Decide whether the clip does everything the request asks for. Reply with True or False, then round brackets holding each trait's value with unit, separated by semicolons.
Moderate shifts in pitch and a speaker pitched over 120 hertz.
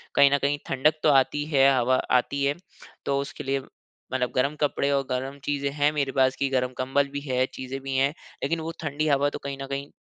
False (1.2 semitones; 140 Hz)